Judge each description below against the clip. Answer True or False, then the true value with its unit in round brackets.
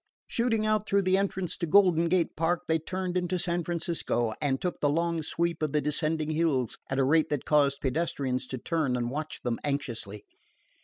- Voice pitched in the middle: True (160 Hz)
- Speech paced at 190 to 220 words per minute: True (195 wpm)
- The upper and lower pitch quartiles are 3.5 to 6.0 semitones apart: True (4.1 semitones)